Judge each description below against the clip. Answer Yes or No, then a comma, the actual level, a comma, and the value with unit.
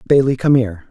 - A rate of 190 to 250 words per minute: Yes, average, 200 wpm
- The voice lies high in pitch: No, low, 120 Hz